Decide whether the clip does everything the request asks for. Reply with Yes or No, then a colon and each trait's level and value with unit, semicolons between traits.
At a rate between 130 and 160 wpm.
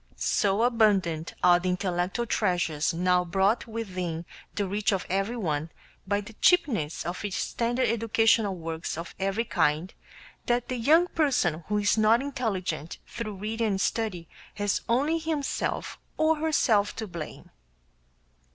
Yes: slow, 135 wpm